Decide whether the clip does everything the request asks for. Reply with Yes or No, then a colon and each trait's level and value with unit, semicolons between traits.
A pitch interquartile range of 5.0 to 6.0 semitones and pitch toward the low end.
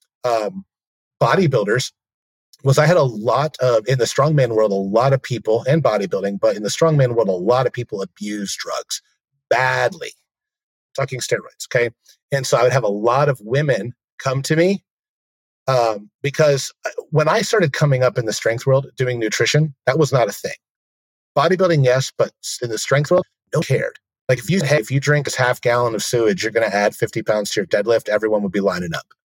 Yes: wide, 5.5 semitones; low, 130 Hz